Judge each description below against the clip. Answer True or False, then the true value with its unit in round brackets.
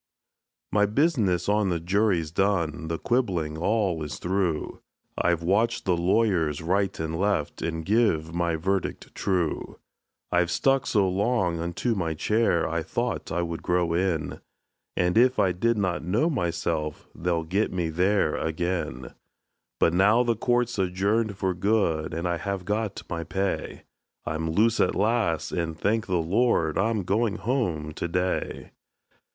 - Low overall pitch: True (90 Hz)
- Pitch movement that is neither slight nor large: True (4.1 semitones)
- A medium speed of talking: True (150 wpm)